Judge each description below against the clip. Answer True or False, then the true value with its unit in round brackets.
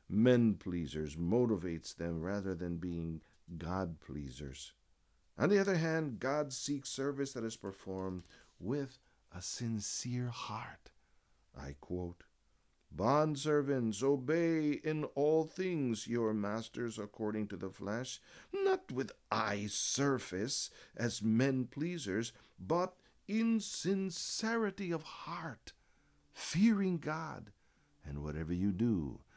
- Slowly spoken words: True (110 wpm)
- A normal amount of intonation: False (8.5 semitones)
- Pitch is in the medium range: False (115 Hz)